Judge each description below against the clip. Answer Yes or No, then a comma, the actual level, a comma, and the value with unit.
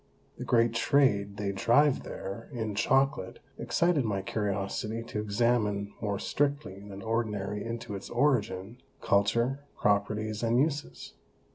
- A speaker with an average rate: No, slow, 125 wpm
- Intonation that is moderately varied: Yes, average, 3.2 semitones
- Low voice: Yes, low, 110 Hz